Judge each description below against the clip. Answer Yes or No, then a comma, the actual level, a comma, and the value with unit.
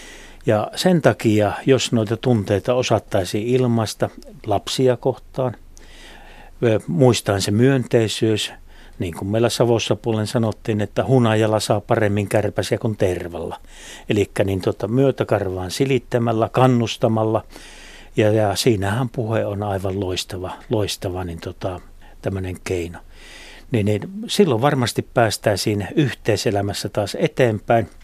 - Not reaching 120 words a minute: Yes, average, 110 wpm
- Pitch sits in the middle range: No, low, 110 Hz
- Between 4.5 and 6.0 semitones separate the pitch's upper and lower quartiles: No, average, 3.7 semitones